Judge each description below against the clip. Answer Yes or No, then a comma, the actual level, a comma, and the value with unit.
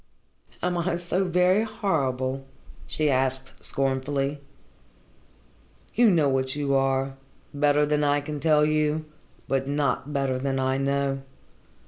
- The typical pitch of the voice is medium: Yes, medium, 145 Hz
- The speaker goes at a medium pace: No, slow, 125 wpm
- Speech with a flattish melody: Yes, narrow, 2.3 semitones